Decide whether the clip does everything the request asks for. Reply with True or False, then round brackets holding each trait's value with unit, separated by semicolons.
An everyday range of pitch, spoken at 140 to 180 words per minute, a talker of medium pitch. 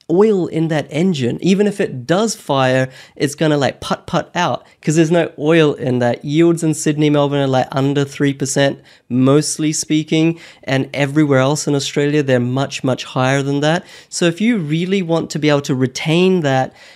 False (3.3 semitones; 190 wpm; 150 Hz)